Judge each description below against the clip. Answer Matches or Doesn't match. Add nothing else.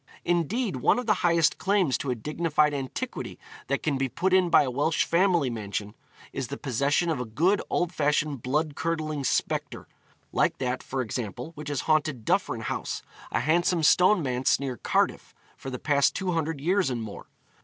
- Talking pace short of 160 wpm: Doesn't match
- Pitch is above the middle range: Doesn't match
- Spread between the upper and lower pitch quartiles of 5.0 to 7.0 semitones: Doesn't match